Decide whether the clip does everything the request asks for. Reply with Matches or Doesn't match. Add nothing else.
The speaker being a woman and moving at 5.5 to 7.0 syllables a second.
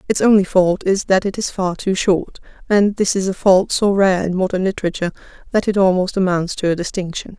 Matches